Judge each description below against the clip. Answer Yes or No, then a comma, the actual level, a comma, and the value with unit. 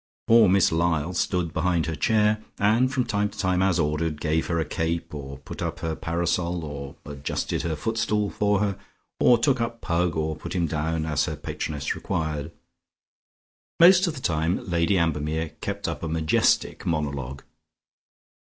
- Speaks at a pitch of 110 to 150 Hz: No, very low, 85 Hz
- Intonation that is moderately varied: Yes, average, 4.3 semitones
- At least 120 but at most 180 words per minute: Yes, average, 170 wpm